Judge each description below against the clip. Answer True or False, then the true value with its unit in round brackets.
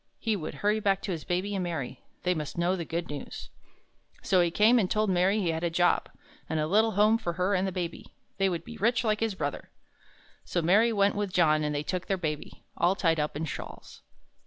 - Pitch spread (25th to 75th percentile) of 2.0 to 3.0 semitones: False (3.7 semitones)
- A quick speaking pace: True (230 wpm)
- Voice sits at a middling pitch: True (180 Hz)